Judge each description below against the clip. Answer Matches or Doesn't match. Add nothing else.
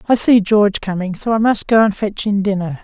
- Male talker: Doesn't match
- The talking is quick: Matches